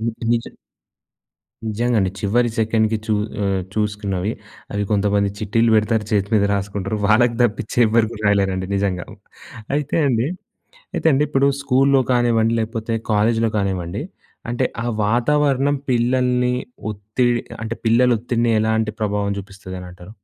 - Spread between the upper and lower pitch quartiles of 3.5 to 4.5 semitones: No, average, 3.0 semitones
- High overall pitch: No, low, 110 Hz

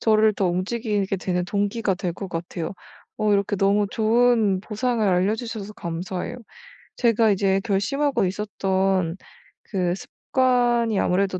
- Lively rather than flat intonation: No, average, 3.1 semitones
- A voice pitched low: No, high, 200 Hz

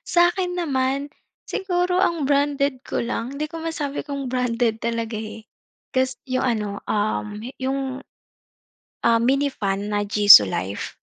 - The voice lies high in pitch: Yes, very high, 260 Hz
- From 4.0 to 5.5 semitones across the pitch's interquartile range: Yes, average, 4.5 semitones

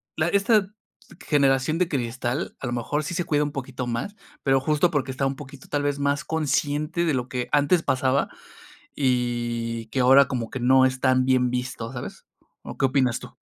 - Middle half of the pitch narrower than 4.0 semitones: Yes, average, 2.7 semitones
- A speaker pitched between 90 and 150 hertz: Yes, low, 135 Hz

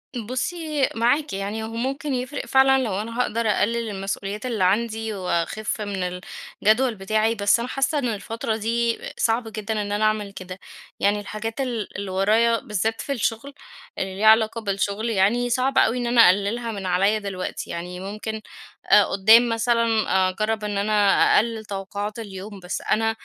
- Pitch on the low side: No, high, 220 Hz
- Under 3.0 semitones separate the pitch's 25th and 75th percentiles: Yes, narrow, 2.6 semitones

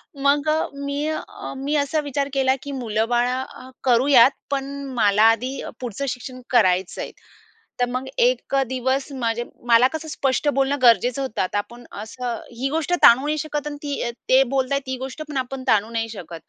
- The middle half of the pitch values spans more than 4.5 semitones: No, average, 3.0 semitones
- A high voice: Yes, very high, 260 Hz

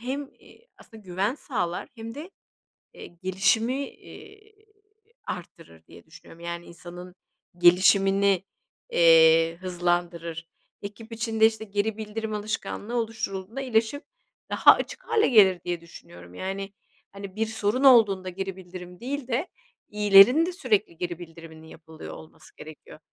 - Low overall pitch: No, high, 195 Hz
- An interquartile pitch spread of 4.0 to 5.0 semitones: Yes, average, 4.5 semitones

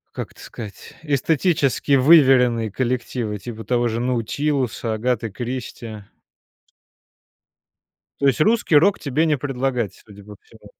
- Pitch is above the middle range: No, low, 125 Hz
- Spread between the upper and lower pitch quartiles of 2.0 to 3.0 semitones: No, average, 3.7 semitones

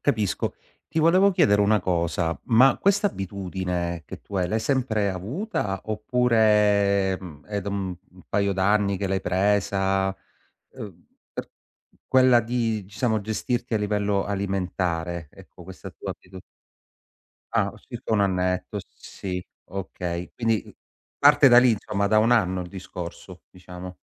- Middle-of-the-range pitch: No, low, 100 Hz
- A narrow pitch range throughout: No, average, 3.2 semitones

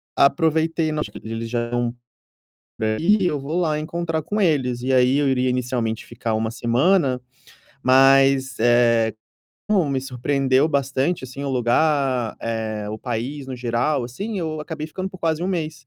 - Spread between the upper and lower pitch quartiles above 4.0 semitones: Yes, average, 4.5 semitones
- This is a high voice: No, low, 135 Hz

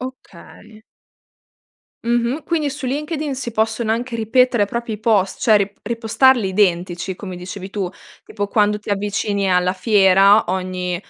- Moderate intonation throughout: Yes, average, 3.7 semitones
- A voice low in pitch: No, high, 210 Hz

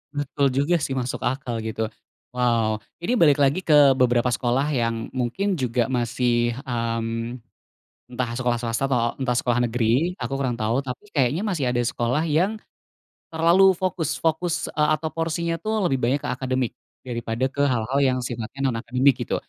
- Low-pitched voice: Yes, low, 130 Hz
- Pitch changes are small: No, average, 3.9 semitones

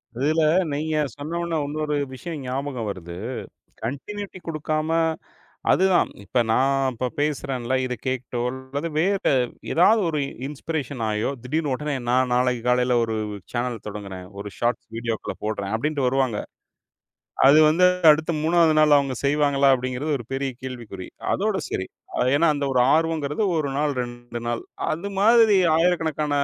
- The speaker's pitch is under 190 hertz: Yes, medium, 140 Hz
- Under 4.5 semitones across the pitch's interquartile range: Yes, average, 4.0 semitones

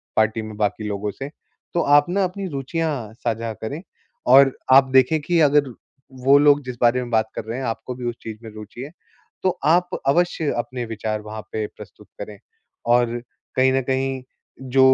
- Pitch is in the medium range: No, low, 130 Hz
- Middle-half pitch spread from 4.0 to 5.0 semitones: Yes, average, 4.4 semitones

